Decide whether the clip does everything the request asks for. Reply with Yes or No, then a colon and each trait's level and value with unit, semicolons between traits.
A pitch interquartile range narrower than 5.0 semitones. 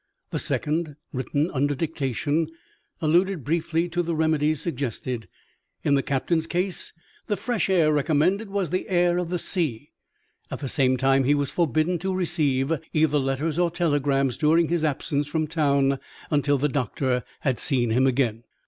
Yes: average, 3.8 semitones